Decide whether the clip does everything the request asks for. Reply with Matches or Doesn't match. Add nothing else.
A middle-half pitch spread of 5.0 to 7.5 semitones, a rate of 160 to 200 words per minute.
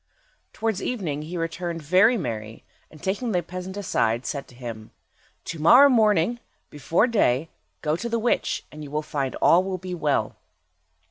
Matches